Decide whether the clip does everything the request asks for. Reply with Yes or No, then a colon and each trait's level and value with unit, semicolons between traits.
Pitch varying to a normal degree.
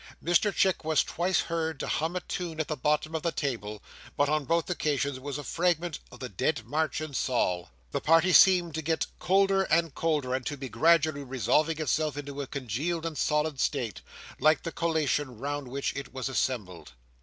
Yes: average, 3.6 semitones